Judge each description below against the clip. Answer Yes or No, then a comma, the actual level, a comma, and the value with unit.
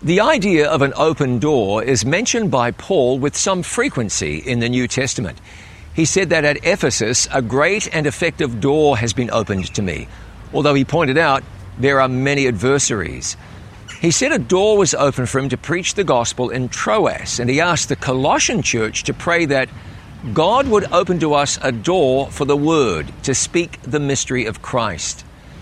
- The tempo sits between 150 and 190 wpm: Yes, average, 185 wpm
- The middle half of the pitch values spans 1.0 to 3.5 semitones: No, average, 4.9 semitones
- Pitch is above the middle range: No, low, 135 Hz